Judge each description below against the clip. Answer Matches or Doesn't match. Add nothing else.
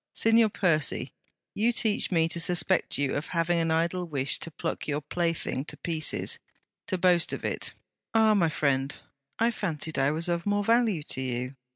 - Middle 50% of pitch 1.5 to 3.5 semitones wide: Doesn't match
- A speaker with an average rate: Matches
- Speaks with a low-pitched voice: Doesn't match